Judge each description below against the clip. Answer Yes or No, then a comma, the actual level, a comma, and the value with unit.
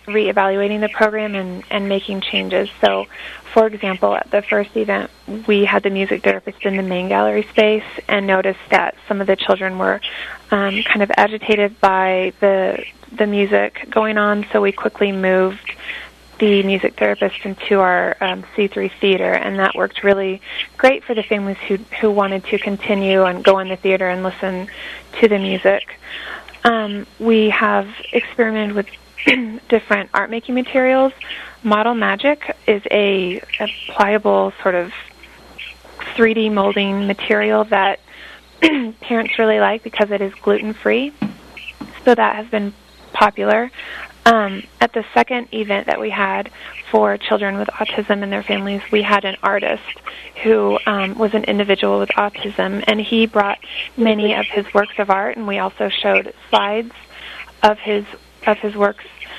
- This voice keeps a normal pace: Yes, average, 160 wpm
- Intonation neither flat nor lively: No, narrow, 1.9 semitones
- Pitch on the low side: No, high, 205 Hz